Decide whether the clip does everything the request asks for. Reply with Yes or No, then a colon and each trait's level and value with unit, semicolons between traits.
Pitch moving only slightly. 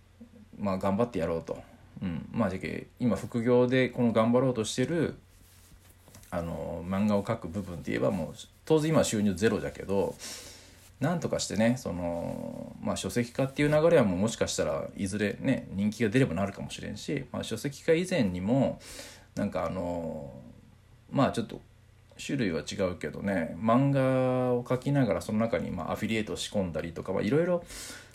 No: wide, 5.4 semitones